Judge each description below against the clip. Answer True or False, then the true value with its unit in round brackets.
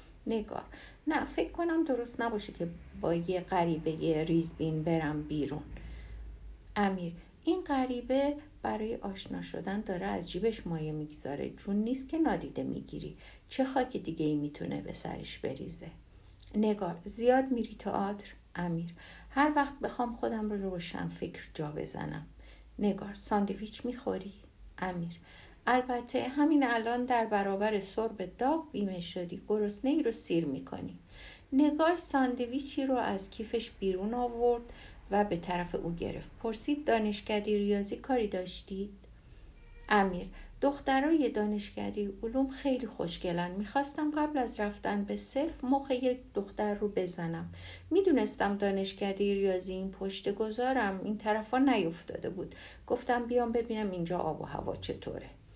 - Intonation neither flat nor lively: False (5.8 semitones)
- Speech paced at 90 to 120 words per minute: False (135 wpm)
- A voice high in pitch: True (210 Hz)